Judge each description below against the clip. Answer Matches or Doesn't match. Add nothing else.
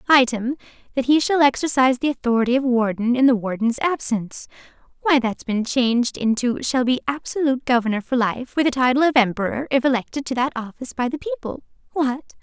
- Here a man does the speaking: Doesn't match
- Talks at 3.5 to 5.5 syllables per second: Doesn't match